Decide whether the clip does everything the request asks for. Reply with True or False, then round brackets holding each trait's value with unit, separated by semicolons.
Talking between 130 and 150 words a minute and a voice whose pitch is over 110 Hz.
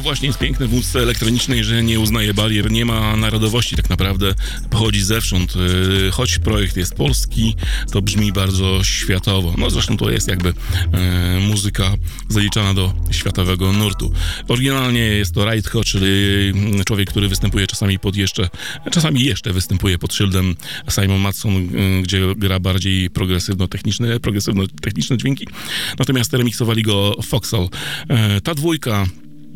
False (140 wpm; 100 Hz)